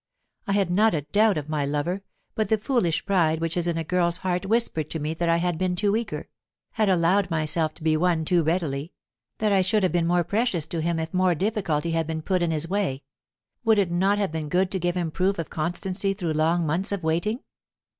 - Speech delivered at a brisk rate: Yes, fast, 235 wpm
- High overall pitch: No, medium, 175 Hz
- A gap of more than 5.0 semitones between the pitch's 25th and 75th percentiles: No, average, 3.4 semitones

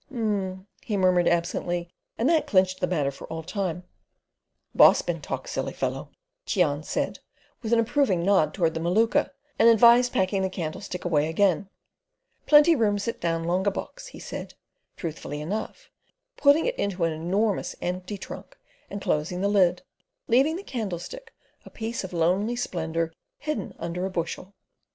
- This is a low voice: No, high, 190 Hz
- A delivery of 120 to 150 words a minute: No, average, 160 wpm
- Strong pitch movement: No, average, 4.8 semitones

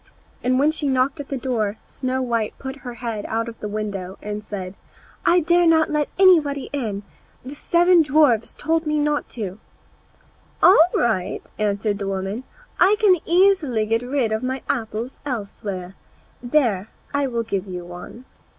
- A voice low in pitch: No, very high, 250 Hz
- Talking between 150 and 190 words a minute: Yes, average, 160 wpm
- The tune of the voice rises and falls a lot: Yes, wide, 5.8 semitones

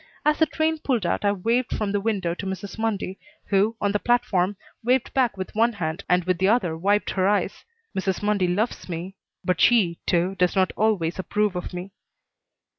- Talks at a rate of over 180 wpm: Yes, average, 195 wpm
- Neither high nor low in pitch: No, high, 200 Hz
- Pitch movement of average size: Yes, average, 3.4 semitones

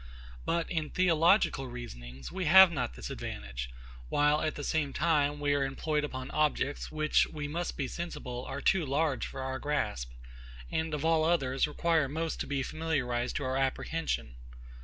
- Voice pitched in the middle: Yes, medium, 145 Hz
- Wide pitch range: No, average, 3.6 semitones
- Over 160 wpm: Yes, average, 170 wpm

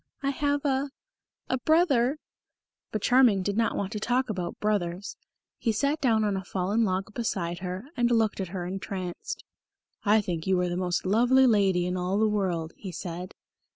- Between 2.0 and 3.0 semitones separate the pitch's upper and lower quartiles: No, average, 4.7 semitones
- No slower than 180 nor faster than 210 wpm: Yes, average, 190 wpm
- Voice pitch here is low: No, high, 205 Hz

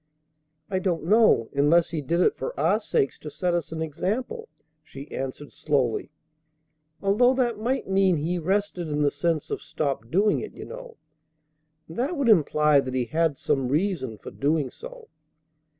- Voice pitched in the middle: Yes, medium, 165 Hz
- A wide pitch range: Yes, wide, 6.2 semitones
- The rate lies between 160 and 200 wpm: Yes, average, 170 wpm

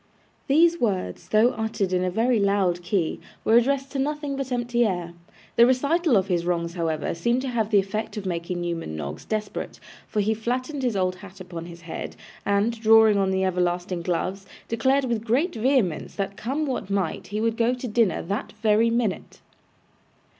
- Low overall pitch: No, high, 215 Hz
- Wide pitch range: No, average, 4.8 semitones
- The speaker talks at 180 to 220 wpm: Yes, average, 185 wpm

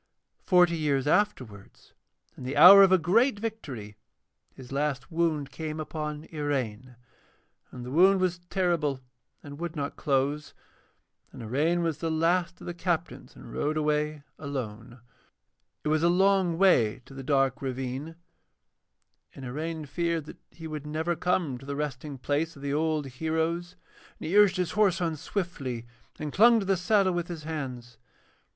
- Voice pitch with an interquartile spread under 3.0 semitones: No, average, 4.1 semitones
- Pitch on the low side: No, medium, 155 Hz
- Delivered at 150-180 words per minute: Yes, average, 160 wpm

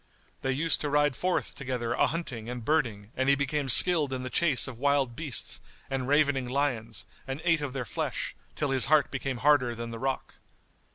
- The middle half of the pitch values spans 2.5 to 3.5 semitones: Yes, average, 3.0 semitones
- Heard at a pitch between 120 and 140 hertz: Yes, low, 135 Hz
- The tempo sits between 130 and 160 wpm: No, average, 195 wpm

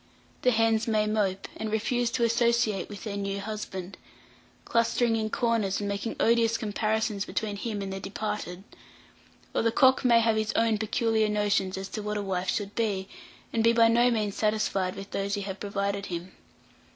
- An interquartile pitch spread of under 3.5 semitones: Yes, narrow, 2.4 semitones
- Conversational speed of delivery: Yes, average, 185 wpm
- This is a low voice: No, high, 215 Hz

